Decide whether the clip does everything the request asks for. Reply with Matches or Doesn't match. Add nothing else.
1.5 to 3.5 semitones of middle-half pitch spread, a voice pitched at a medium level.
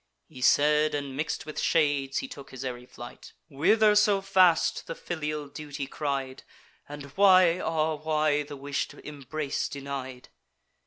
Matches